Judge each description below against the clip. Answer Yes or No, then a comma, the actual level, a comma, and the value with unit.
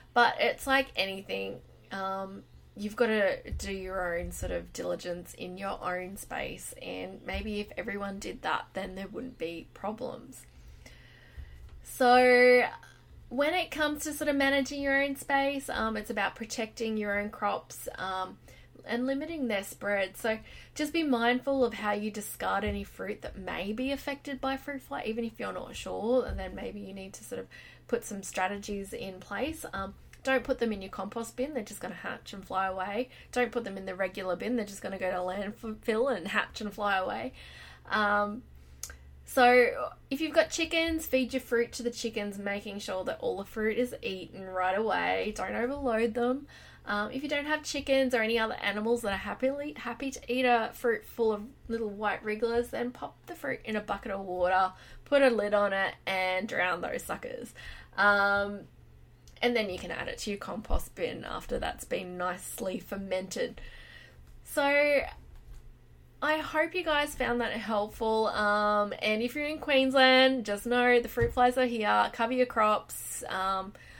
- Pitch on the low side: No, high, 220 Hz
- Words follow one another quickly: No, average, 185 wpm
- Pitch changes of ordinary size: Yes, average, 4.8 semitones